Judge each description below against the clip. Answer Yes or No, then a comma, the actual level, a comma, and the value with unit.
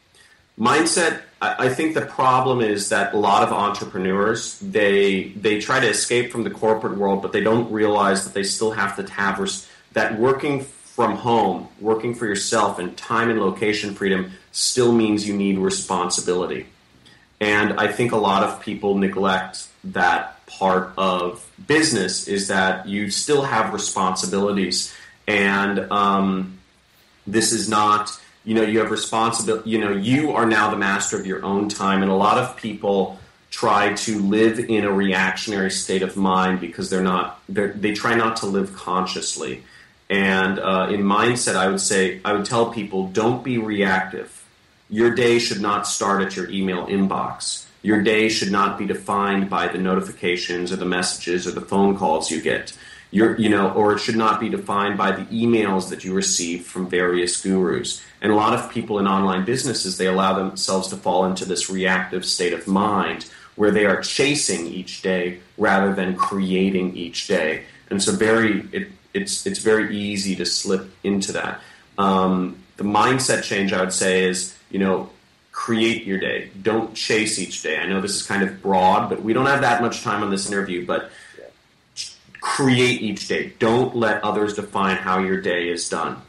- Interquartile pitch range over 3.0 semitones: No, narrow, 2.5 semitones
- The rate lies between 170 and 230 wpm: Yes, average, 180 wpm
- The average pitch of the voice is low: Yes, low, 100 Hz